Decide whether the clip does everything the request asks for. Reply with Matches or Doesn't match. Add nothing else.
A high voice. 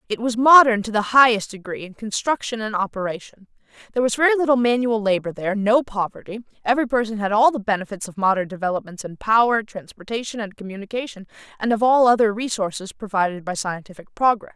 Matches